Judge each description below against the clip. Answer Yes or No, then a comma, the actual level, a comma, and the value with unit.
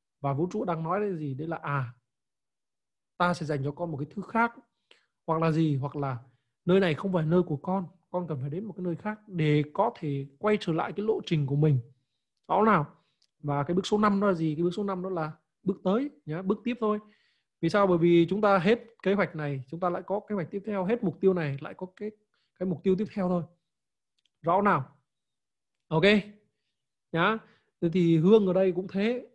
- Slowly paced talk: No, average, 235 wpm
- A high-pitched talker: No, medium, 180 Hz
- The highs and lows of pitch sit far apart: No, average, 5.0 semitones